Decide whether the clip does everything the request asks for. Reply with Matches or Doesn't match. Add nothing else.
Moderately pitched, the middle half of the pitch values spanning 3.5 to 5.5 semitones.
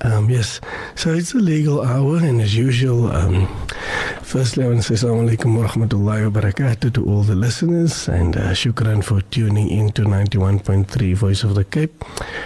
Doesn't match